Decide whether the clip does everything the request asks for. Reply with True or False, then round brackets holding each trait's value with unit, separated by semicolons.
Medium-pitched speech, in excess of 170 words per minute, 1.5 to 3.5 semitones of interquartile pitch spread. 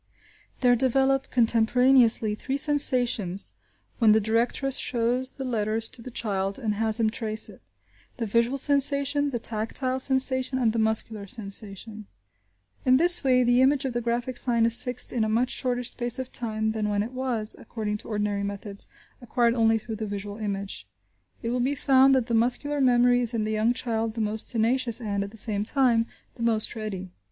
False (230 Hz; 185 wpm; 2.9 semitones)